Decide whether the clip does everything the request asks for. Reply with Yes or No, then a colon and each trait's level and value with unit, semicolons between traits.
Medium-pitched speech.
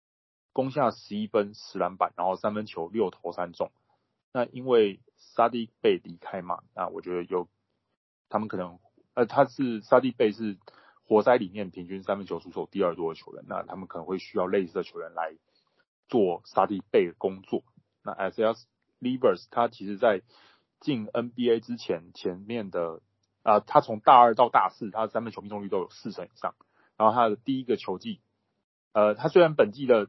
No: low, 110 Hz